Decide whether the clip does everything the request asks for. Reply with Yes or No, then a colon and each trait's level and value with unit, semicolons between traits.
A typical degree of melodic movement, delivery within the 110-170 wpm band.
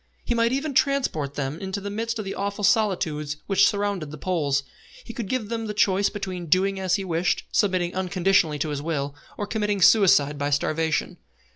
No: average, 4.8 semitones; average, 190 wpm